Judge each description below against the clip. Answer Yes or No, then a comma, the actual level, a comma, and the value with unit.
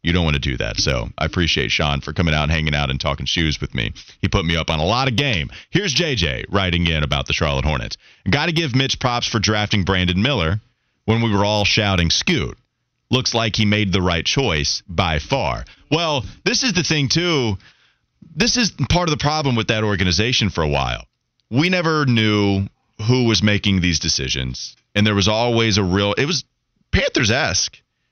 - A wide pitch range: Yes, wide, 7.3 semitones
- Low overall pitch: Yes, low, 105 Hz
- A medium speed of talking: No, fast, 210 wpm